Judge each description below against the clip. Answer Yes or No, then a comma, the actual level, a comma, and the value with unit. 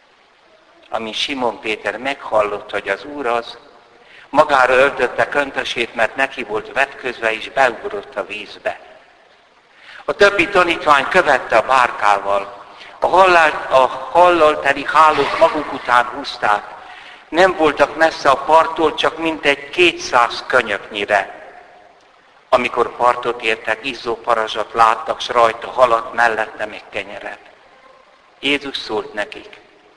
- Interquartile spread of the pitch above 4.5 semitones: Yes, average, 5.2 semitones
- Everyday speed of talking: Yes, average, 115 wpm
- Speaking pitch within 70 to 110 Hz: No, low, 130 Hz